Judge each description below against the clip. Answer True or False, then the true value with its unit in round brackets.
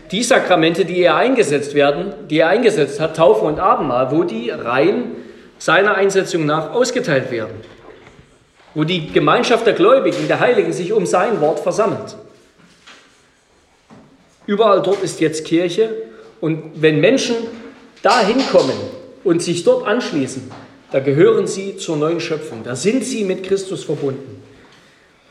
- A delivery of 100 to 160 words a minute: True (140 wpm)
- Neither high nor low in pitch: True (175 Hz)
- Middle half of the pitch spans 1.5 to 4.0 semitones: False (5.1 semitones)